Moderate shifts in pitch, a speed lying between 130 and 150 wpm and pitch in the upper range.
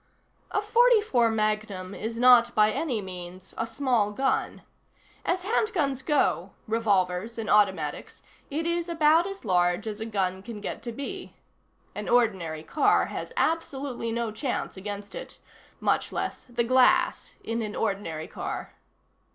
No: wide, 5.8 semitones; average, 145 wpm; high, 230 Hz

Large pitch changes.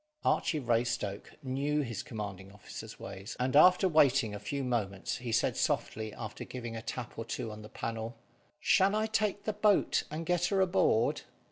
Yes: wide, 6.5 semitones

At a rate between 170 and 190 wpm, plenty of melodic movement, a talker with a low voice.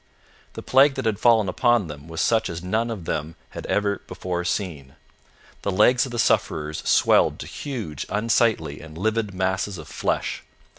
Yes: average, 175 wpm; wide, 5.8 semitones; low, 100 Hz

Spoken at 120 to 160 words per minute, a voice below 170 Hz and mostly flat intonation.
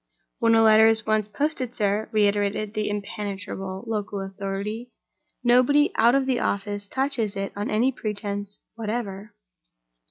No: slow, 135 wpm; high, 215 Hz; narrow, 2.2 semitones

